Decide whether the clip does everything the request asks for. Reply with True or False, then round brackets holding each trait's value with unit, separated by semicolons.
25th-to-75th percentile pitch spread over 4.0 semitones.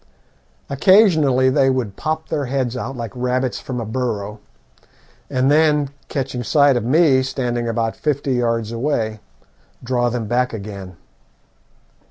False (3.0 semitones)